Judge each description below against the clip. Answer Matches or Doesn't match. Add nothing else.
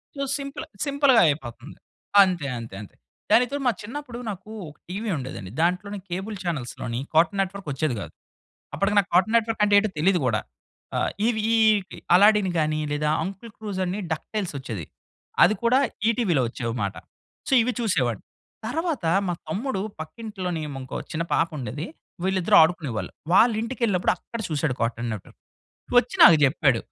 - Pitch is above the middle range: Doesn't match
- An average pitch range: Doesn't match